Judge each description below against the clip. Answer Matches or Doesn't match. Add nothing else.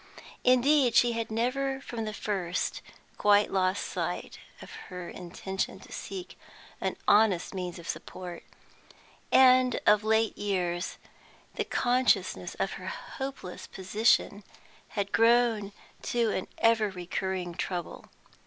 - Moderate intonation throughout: Matches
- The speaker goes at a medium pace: Doesn't match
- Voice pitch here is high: Matches